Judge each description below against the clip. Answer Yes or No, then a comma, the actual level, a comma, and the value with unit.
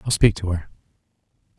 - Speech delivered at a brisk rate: No, average, 150 wpm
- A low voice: Yes, very low, 95 Hz